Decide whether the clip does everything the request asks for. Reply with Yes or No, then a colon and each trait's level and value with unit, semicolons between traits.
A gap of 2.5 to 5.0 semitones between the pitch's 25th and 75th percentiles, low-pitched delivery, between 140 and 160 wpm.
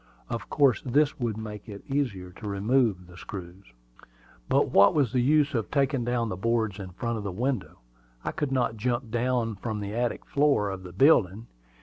No: average, 4.2 semitones; low, 115 Hz; average, 195 wpm